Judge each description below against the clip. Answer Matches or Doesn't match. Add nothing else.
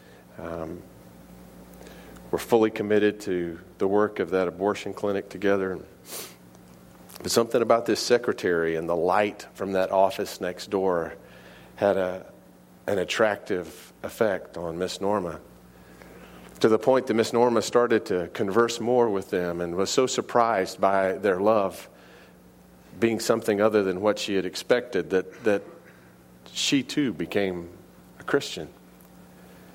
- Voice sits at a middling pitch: Doesn't match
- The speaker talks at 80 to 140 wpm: Matches